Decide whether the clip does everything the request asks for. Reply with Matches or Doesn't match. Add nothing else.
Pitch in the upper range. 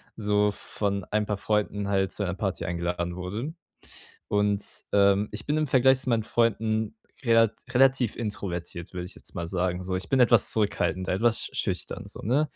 Doesn't match